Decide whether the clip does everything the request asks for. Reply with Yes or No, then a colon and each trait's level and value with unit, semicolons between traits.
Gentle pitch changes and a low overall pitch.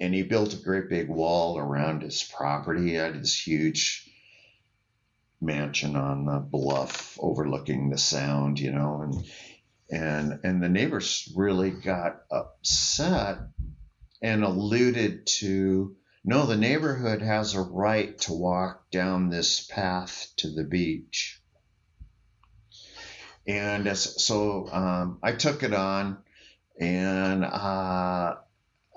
No: average, 4.8 semitones; very low, 95 Hz